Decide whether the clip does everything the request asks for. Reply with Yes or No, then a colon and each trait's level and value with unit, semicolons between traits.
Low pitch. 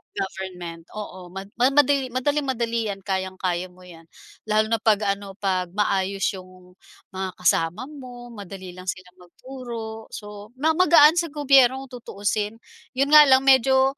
No: high, 210 Hz